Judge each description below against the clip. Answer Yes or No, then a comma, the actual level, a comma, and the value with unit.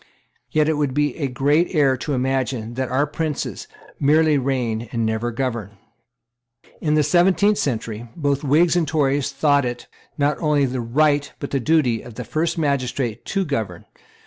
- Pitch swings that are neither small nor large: Yes, average, 3.8 semitones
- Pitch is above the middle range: No, medium, 140 Hz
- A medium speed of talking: Yes, average, 170 wpm